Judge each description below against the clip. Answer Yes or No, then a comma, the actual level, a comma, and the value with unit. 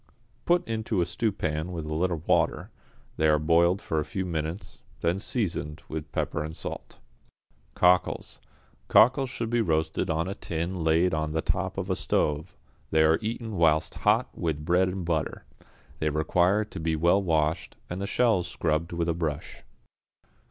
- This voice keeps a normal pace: Yes, average, 170 wpm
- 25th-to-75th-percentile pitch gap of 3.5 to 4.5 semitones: No, average, 3.1 semitones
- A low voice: Yes, very low, 85 Hz